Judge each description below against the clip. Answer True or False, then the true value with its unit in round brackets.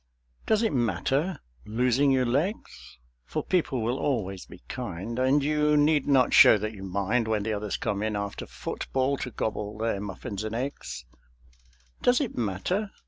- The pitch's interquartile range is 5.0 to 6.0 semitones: True (5.3 semitones)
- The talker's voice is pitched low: True (120 Hz)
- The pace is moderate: True (165 wpm)